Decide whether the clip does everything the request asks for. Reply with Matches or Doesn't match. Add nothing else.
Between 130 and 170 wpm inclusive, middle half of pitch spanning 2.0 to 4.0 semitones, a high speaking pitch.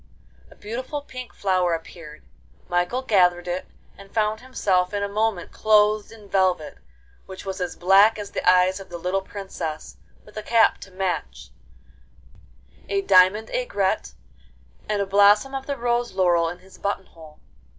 Matches